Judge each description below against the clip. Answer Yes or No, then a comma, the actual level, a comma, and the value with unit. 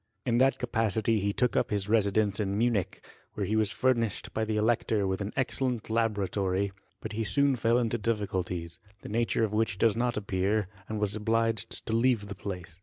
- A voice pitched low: Yes, low, 110 Hz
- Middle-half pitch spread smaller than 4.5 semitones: Yes, narrow, 2.4 semitones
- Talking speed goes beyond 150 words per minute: Yes, average, 195 wpm